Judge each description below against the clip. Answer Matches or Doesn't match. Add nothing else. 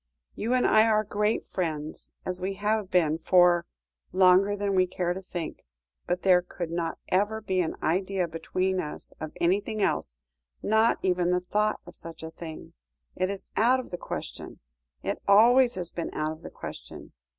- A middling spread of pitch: Matches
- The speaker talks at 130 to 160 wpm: Doesn't match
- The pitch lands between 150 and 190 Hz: Matches